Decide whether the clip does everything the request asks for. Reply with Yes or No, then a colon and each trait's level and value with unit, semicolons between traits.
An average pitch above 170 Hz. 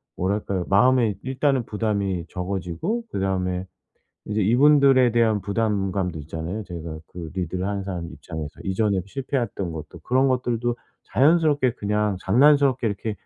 No: low, 105 Hz